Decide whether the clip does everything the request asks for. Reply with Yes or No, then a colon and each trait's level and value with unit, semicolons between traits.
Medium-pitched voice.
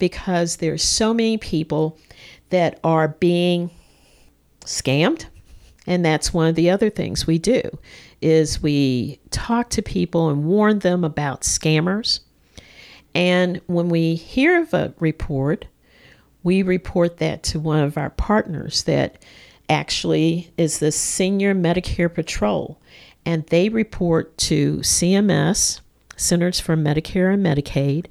Yes: medium, 165 Hz